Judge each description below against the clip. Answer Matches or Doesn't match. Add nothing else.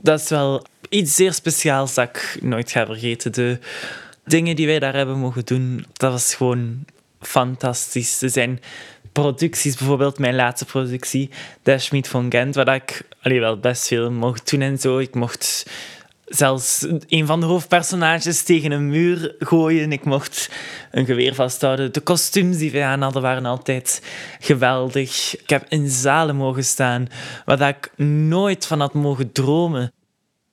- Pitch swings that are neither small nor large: Matches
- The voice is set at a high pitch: Doesn't match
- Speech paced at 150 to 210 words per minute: Matches